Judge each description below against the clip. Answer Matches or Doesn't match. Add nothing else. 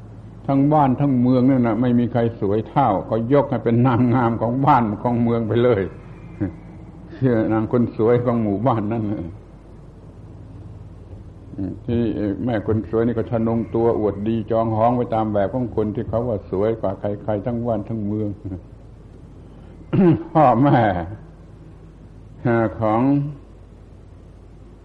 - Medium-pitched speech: Doesn't match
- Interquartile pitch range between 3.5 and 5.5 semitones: Doesn't match